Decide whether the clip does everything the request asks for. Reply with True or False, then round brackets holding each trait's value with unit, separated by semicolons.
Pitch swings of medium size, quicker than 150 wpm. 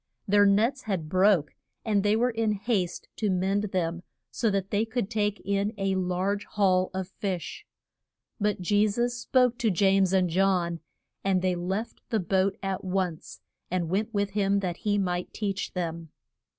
False (2.2 semitones; 170 wpm)